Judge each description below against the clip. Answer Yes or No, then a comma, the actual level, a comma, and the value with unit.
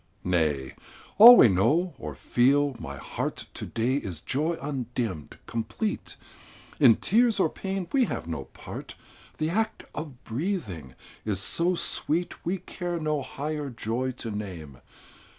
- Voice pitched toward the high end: No, low, 135 Hz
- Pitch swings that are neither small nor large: No, wide, 8.6 semitones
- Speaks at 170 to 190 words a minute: No, average, 140 wpm